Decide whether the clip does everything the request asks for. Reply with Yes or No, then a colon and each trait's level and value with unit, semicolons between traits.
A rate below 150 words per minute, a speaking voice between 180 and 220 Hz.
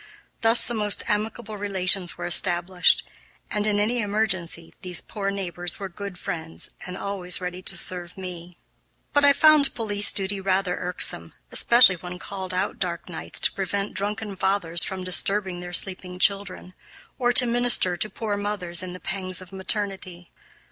No: average, 160 wpm; high, 190 Hz